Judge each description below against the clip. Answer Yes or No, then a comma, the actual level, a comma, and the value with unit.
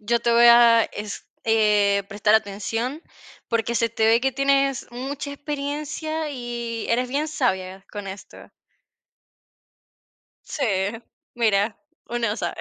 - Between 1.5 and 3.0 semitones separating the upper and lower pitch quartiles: No, average, 4.4 semitones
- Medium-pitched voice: No, high, 235 Hz